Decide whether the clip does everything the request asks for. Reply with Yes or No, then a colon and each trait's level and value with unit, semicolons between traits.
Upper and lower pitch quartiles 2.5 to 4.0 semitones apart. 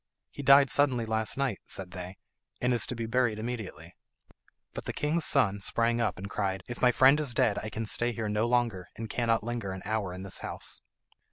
Yes: average, 3.6 semitones